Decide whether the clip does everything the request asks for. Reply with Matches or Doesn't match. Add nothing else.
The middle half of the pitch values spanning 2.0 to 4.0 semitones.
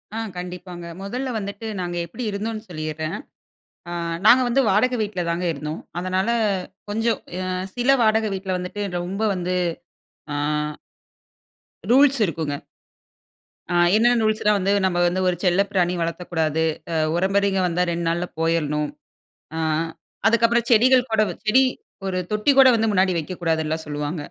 Doesn't match